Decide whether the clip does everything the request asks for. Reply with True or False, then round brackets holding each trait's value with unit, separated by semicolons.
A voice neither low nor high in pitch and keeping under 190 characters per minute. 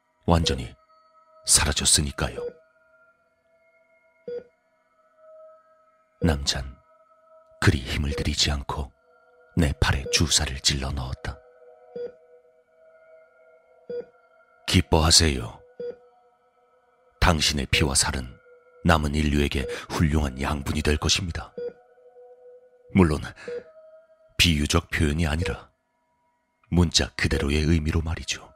True (160 Hz; 175 characters per minute)